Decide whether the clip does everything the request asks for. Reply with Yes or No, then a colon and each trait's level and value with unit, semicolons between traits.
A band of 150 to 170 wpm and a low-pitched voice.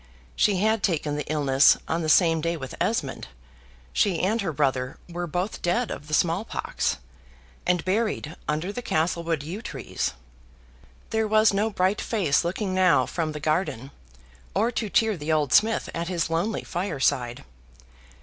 No: average, 160 wpm; medium, 170 Hz